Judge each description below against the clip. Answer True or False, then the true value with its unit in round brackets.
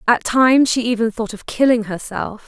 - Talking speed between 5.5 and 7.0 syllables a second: False (5.2 syllables/s)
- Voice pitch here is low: False (230 Hz)